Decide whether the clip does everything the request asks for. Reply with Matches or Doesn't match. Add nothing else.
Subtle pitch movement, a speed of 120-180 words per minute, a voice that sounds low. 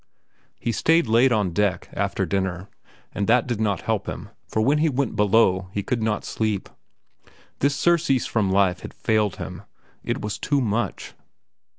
Doesn't match